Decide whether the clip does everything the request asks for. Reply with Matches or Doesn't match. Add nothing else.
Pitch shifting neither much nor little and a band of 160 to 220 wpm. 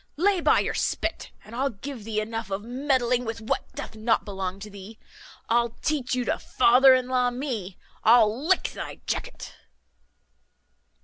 Matches